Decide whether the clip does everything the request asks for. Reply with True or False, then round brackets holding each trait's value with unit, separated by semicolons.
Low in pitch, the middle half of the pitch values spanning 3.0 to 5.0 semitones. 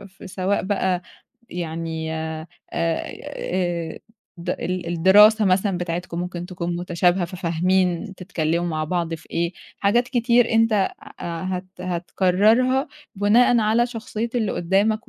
False (185 Hz; 3.4 semitones)